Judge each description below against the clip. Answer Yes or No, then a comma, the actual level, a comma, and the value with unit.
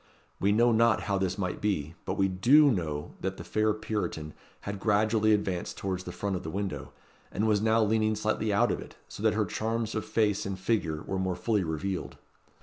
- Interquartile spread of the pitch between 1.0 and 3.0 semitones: Yes, narrow, 2.6 semitones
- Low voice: Yes, low, 100 Hz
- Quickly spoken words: Yes, fast, 210 wpm